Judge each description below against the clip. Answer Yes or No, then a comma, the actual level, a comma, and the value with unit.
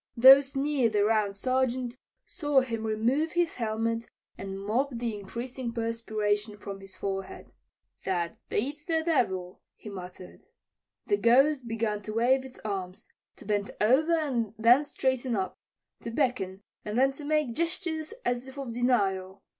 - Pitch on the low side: No, high, 235 Hz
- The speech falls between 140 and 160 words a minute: Yes, average, 150 wpm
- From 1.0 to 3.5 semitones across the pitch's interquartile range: No, average, 4.5 semitones